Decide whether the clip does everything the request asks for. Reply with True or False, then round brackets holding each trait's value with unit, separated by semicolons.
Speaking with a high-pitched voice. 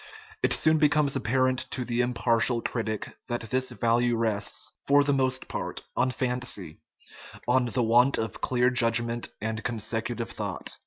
False (120 Hz)